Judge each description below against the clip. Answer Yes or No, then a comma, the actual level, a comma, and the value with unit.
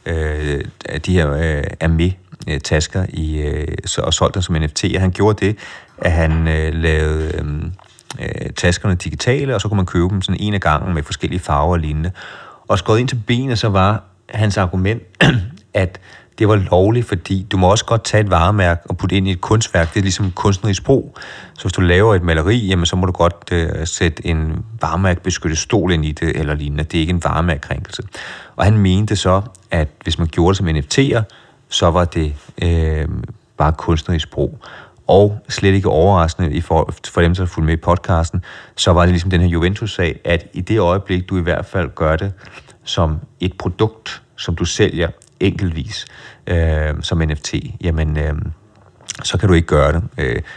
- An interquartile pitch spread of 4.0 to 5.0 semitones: No, average, 3.4 semitones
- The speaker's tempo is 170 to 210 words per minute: Yes, average, 190 wpm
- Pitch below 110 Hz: Yes, very low, 90 Hz